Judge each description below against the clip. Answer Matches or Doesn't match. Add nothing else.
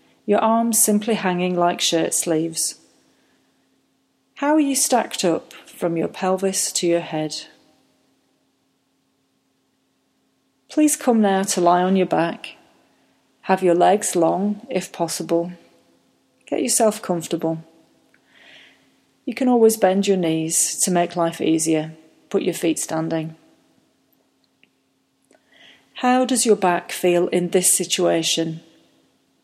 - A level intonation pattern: Doesn't match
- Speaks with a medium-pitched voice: Matches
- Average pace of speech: Doesn't match